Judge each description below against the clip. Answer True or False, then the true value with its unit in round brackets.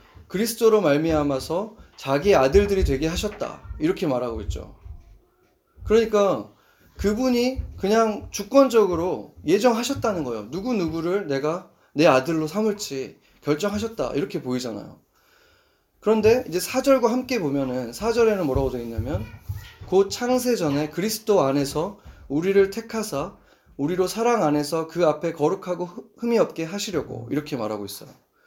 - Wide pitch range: True (7.4 semitones)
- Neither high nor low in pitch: False (195 Hz)